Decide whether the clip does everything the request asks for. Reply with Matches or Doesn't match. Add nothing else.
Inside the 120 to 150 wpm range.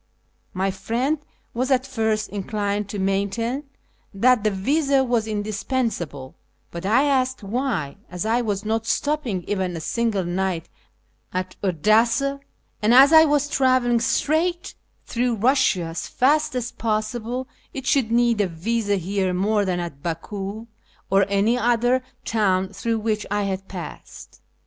Matches